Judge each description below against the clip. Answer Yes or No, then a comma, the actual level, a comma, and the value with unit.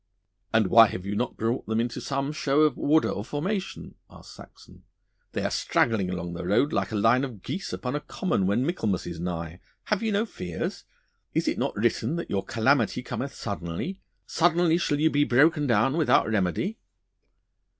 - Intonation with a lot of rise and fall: Yes, wide, 7.3 semitones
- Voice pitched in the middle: No, low, 125 Hz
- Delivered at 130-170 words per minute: No, average, 185 wpm